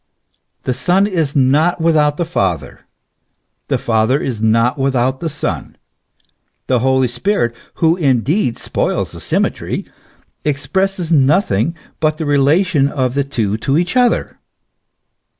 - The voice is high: No, medium, 140 Hz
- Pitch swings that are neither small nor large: Yes, average, 4.6 semitones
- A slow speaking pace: Yes, slow, 125 wpm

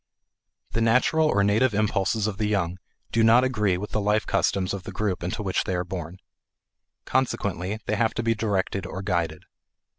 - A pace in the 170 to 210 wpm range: Yes, average, 185 wpm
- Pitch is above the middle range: No, low, 100 Hz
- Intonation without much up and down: No, average, 3.2 semitones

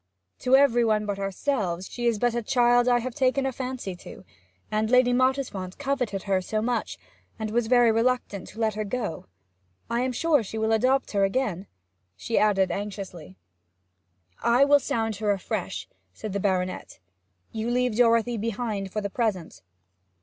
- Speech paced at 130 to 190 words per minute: Yes, average, 170 wpm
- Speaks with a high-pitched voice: Yes, high, 225 Hz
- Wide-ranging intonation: No, average, 3.6 semitones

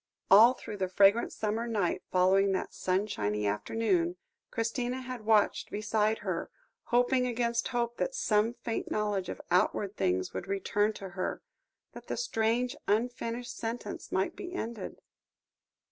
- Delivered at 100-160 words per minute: Yes, average, 140 wpm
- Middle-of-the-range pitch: No, high, 220 Hz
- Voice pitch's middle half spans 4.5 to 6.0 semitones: No, average, 3.4 semitones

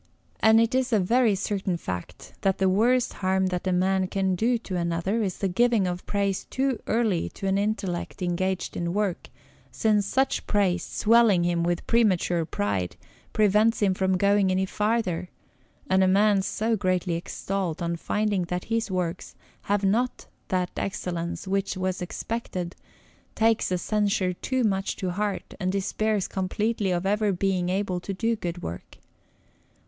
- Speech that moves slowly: No, average, 165 wpm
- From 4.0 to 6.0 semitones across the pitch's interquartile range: No, average, 2.8 semitones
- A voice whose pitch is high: Yes, high, 195 Hz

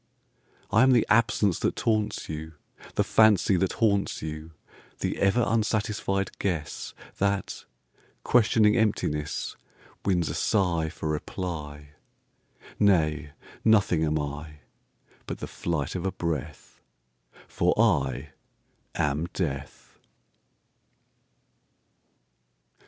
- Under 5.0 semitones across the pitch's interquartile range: No, average, 5.3 semitones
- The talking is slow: Yes, slow, 80 wpm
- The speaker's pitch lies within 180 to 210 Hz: No, very low, 85 Hz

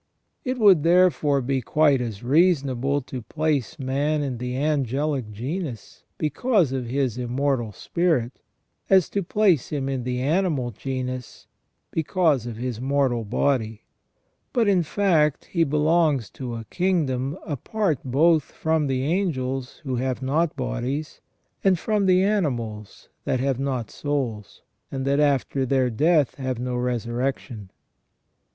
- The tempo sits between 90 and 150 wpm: Yes, average, 140 wpm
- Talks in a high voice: No, low, 135 Hz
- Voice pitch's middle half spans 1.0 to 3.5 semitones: No, average, 4.1 semitones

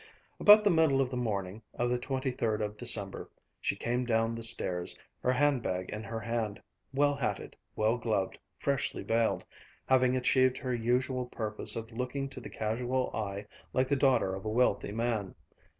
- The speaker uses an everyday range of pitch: Yes, average, 3.0 semitones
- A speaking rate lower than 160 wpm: No, average, 180 wpm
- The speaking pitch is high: No, low, 120 Hz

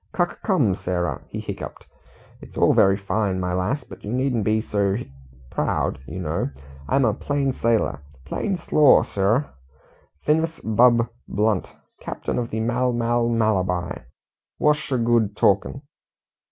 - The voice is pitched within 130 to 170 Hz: No, low, 115 Hz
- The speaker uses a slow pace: No, average, 145 wpm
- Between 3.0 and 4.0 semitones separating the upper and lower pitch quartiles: No, average, 4.8 semitones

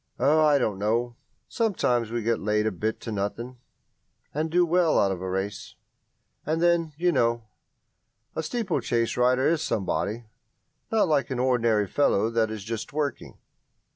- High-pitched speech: No, low, 120 Hz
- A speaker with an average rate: Yes, average, 160 wpm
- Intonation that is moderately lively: No, wide, 6.0 semitones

